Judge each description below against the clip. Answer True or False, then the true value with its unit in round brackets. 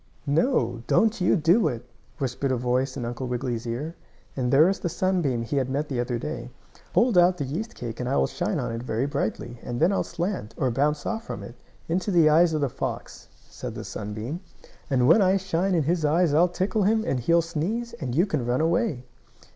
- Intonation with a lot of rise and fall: True (6.3 semitones)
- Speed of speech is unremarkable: False (220 wpm)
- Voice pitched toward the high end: False (150 Hz)